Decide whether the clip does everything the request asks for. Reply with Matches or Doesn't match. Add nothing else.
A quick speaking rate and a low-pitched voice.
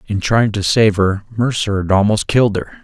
Matches